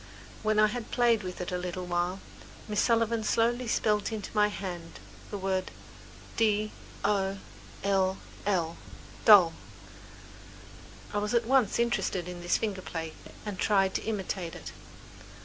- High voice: Yes, high, 205 Hz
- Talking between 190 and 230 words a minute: No, average, 140 wpm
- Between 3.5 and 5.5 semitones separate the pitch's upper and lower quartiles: No, average, 3.1 semitones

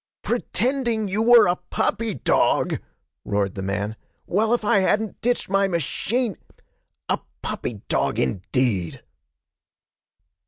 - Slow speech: Yes, slow, 115 wpm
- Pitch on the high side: Yes, high, 195 Hz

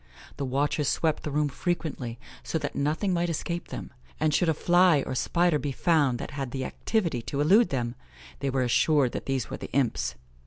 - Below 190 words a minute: No, average, 195 wpm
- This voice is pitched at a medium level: Yes, medium, 145 Hz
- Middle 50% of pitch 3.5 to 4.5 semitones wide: Yes, average, 4.1 semitones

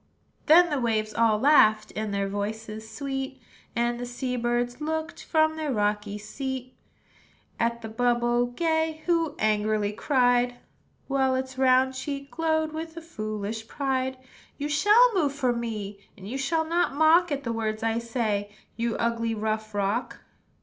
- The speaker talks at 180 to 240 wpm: No, average, 155 wpm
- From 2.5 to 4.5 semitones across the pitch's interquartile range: No, average, 5.0 semitones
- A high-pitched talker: Yes, high, 245 Hz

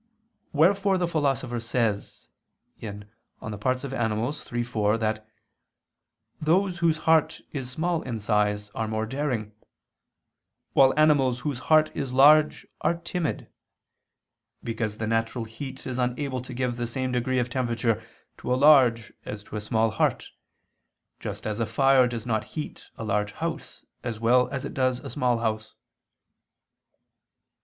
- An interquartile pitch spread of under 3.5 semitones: No, average, 4.1 semitones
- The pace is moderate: Yes, average, 145 wpm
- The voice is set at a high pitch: No, low, 125 Hz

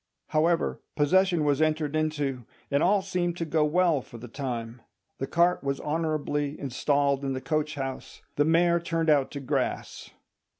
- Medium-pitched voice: Yes, medium, 150 Hz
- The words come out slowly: No, average, 165 wpm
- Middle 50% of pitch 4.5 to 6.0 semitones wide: No, average, 3.1 semitones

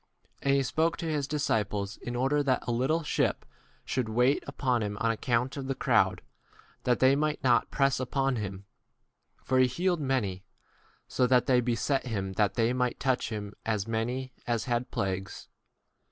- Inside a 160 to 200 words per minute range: Yes, average, 185 wpm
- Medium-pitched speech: No, low, 125 Hz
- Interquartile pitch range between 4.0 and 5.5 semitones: No, average, 3.3 semitones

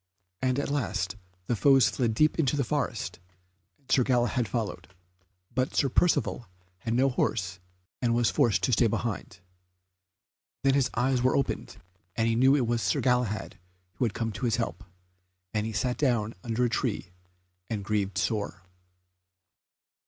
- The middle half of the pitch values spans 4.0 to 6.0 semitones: No, average, 3.2 semitones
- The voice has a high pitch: No, low, 120 Hz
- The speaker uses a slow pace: No, average, 160 wpm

